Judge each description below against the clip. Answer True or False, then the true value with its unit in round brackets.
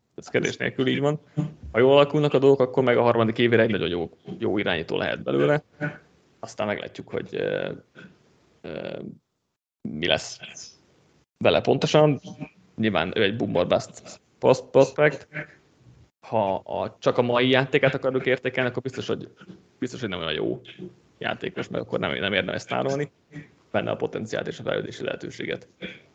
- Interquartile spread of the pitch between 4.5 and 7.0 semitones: False (2.9 semitones)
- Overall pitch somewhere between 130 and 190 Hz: True (135 Hz)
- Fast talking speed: False (145 wpm)